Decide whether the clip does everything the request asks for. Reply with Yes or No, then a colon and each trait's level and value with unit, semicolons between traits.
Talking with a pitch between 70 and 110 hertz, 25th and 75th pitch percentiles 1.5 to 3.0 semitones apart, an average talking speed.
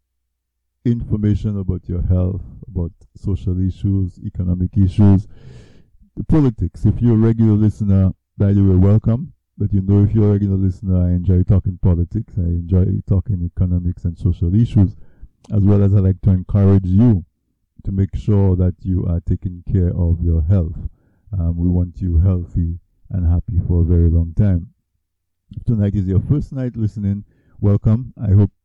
Yes: very low, 95 Hz; narrow, 2.6 semitones; average, 170 wpm